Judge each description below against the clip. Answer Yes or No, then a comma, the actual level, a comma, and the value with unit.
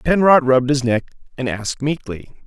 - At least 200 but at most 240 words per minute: No, average, 170 wpm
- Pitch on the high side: No, low, 135 Hz